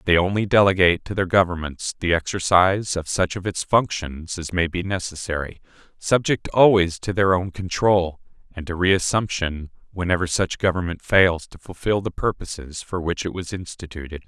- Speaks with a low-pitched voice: Yes, very low, 90 Hz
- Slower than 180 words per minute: Yes, average, 165 wpm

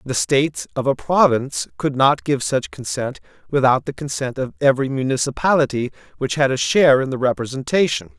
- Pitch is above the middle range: No, low, 130 Hz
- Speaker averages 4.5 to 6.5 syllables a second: Yes, 5.7 syllables/s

